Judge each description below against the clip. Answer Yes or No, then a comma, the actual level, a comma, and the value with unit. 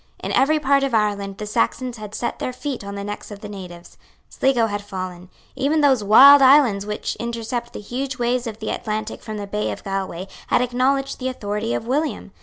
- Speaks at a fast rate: Yes, fast, 210 wpm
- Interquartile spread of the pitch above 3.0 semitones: Yes, average, 4.2 semitones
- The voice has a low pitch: No, high, 225 Hz